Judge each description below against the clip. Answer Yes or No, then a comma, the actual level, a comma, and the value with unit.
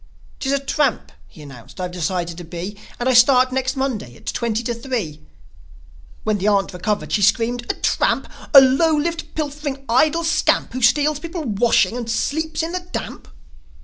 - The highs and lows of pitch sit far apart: Yes, wide, 6.4 semitones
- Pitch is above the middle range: Yes, high, 245 Hz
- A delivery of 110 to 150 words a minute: No, average, 180 wpm